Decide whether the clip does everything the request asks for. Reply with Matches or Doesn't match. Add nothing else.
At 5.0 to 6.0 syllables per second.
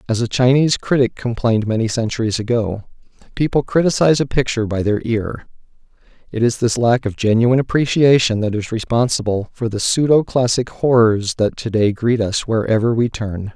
Matches